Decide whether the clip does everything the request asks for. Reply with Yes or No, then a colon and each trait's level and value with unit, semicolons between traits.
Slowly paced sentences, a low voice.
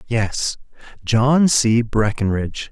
Yes: slow, 90 wpm; low, 115 Hz